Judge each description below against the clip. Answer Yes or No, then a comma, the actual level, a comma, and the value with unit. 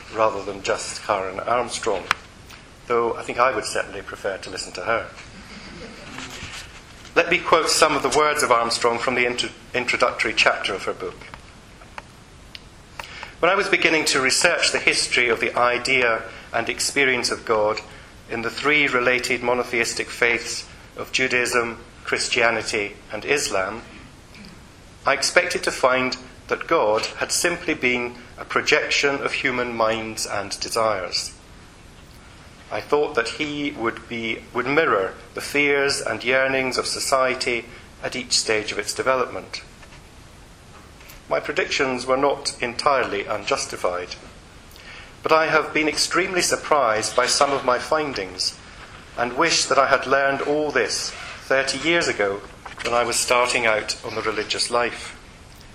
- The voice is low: Yes, low, 125 Hz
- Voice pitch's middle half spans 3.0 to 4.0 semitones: Yes, average, 3.4 semitones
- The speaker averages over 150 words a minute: No, average, 140 wpm